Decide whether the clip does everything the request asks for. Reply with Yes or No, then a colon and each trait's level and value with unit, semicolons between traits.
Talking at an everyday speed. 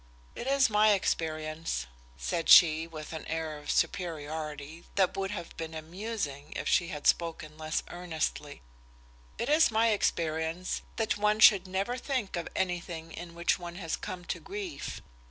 Yes: average, 155 wpm